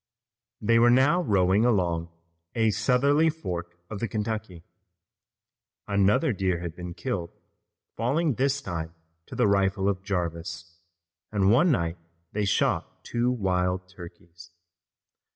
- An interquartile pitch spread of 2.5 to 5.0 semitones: No, wide, 5.4 semitones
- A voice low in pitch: Yes, low, 100 Hz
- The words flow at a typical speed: No, slow, 125 wpm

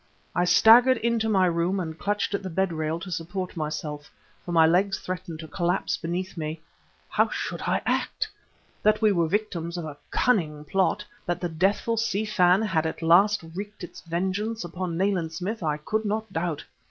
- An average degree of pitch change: Yes, average, 3.9 semitones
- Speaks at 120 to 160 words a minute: No, average, 185 wpm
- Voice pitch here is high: No, medium, 180 Hz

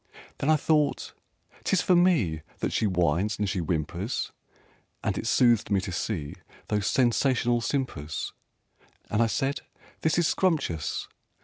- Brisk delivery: No, average, 140 wpm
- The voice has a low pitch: Yes, low, 110 Hz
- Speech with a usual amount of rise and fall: No, wide, 7.8 semitones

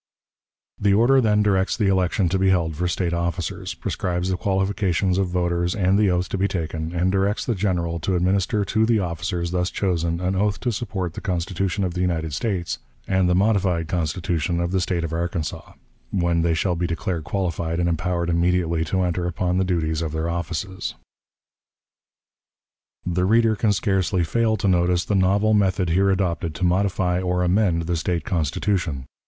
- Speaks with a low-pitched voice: Yes, very low, 90 Hz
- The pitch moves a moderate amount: No, narrow, 2.2 semitones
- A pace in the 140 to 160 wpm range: No, average, 180 wpm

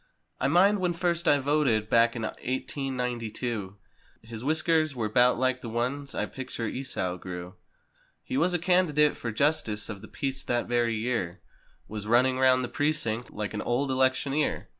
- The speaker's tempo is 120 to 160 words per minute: No, average, 175 wpm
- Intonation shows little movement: No, average, 4.4 semitones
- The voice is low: Yes, low, 130 Hz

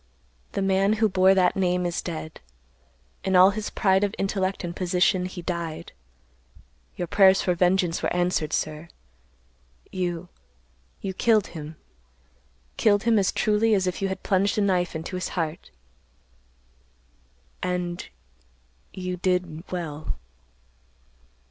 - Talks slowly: Yes, slow, 120 wpm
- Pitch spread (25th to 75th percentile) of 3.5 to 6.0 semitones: No, narrow, 2.5 semitones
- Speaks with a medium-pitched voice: Yes, medium, 180 Hz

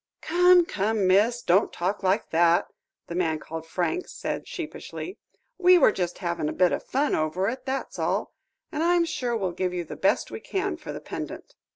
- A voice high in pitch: Yes, high, 205 Hz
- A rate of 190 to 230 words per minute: Yes, average, 195 wpm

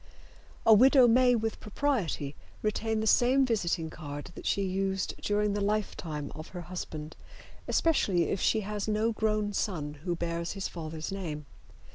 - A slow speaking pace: No, average, 155 wpm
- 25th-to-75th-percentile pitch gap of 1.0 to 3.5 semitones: No, average, 4.6 semitones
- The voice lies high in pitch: Yes, high, 195 Hz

